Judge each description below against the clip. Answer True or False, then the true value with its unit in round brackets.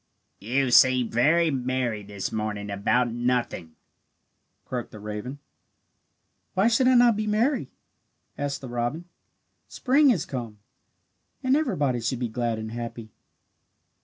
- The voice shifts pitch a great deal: True (6.8 semitones)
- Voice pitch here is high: False (125 Hz)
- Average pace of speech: False (130 wpm)